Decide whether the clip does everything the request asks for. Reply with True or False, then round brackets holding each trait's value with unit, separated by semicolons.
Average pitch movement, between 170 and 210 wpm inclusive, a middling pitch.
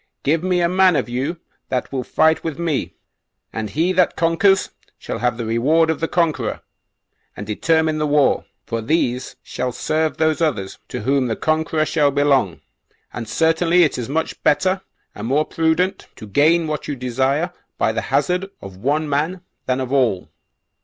True (4.5 semitones; 175 wpm; 150 Hz)